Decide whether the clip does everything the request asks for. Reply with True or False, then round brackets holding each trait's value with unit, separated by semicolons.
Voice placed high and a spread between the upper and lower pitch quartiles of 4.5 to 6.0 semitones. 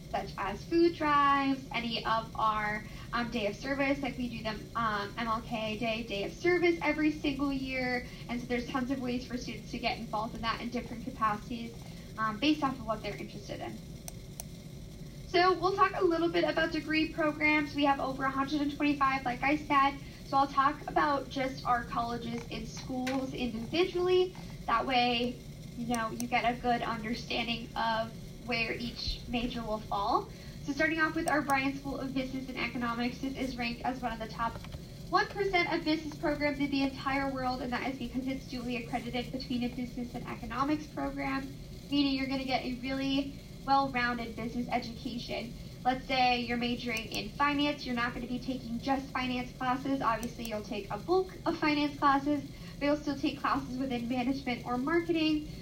False (255 Hz; 3.3 semitones)